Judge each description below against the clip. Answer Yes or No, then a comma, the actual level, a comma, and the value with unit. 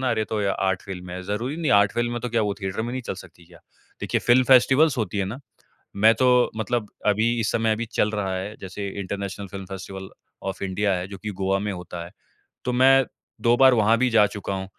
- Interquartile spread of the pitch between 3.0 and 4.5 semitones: Yes, average, 3.6 semitones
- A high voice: No, low, 105 Hz